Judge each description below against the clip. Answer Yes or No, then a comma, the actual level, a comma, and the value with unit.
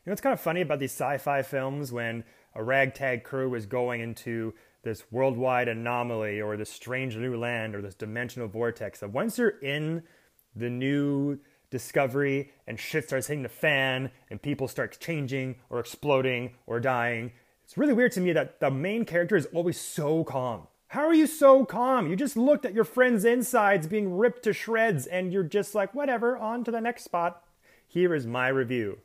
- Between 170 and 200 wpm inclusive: Yes, average, 195 wpm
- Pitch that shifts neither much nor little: No, wide, 8.1 semitones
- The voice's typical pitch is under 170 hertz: Yes, medium, 140 Hz